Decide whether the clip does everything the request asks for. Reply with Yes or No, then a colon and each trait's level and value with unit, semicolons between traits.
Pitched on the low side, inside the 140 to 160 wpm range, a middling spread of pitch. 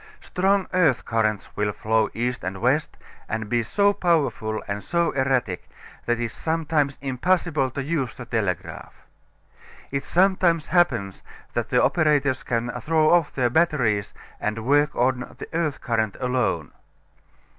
No: low, 130 Hz; average, 145 wpm; wide, 6.3 semitones